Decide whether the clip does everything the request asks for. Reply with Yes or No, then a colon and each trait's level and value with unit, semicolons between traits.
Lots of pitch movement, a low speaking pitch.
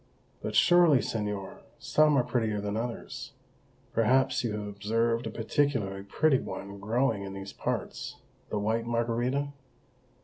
No: average, 4.2 semitones; low, 115 Hz